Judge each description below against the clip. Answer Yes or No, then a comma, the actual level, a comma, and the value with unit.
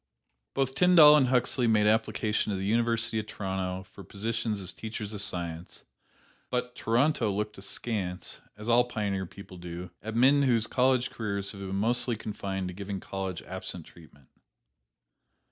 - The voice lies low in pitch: Yes, low, 105 Hz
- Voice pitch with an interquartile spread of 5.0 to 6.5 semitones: No, average, 3.8 semitones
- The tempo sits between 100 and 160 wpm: Yes, average, 155 wpm